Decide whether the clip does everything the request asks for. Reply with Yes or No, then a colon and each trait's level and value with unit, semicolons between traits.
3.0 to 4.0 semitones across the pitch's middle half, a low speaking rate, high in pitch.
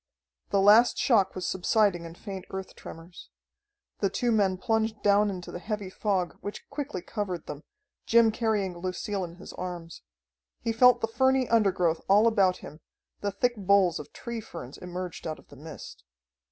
No: average, 3.7 semitones; average, 170 wpm; high, 195 Hz